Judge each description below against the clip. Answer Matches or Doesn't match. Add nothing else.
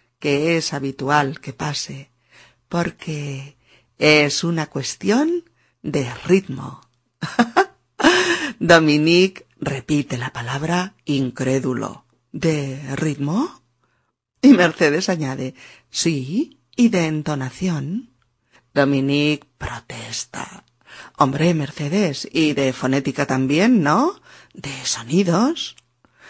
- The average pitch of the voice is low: Doesn't match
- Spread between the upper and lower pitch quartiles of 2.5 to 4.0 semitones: Doesn't match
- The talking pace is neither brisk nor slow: Doesn't match